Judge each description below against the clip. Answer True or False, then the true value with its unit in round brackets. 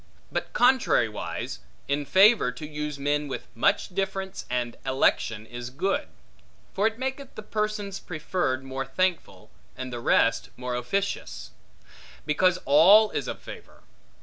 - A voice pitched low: False (150 Hz)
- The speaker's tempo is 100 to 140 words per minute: True (135 wpm)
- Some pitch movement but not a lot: False (7.7 semitones)